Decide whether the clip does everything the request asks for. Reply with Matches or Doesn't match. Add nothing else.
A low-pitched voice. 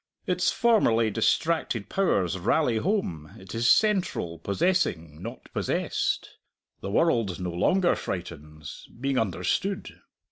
Matches